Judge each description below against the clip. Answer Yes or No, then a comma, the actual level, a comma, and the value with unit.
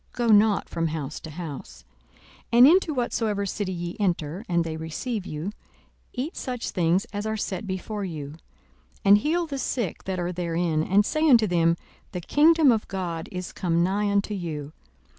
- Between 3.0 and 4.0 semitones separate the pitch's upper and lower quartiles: No, average, 4.7 semitones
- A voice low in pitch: No, high, 190 Hz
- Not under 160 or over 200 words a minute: Yes, average, 180 wpm